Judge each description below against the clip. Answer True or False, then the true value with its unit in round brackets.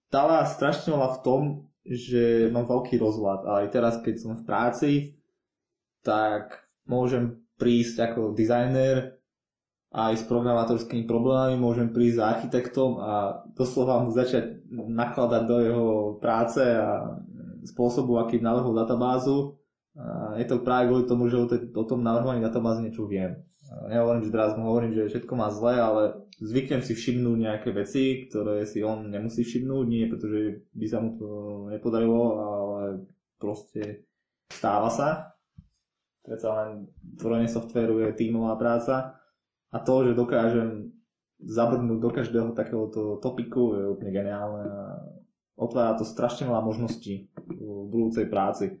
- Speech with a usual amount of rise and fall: False (2.3 semitones)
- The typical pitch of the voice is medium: False (115 Hz)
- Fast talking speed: False (140 wpm)